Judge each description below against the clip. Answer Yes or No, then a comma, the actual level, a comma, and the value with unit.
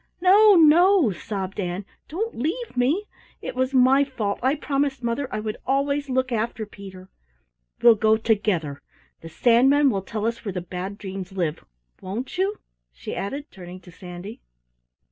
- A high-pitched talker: Yes, high, 230 Hz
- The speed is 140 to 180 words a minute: Yes, average, 160 wpm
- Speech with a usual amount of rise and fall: No, wide, 6.5 semitones